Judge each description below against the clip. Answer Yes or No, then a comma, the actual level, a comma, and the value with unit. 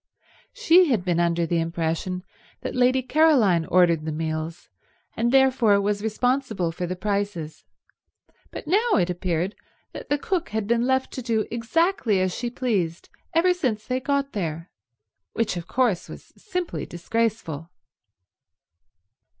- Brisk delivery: No, average, 140 wpm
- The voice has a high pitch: Yes, high, 215 Hz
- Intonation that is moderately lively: No, wide, 7.2 semitones